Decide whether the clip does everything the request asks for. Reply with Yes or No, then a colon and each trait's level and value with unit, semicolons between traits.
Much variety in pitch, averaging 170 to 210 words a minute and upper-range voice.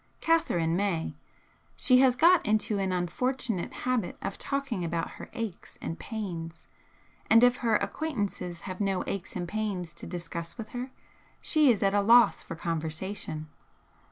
No: wide, 6.0 semitones; average, 155 wpm; high, 200 Hz